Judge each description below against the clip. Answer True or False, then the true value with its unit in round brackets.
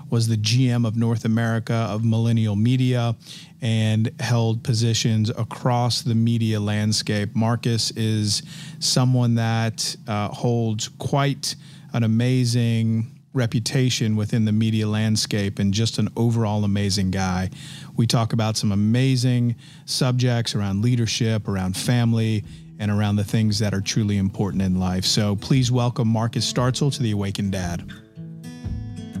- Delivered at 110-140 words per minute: True (135 wpm)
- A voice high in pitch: False (115 Hz)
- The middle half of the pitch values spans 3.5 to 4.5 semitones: False (2.8 semitones)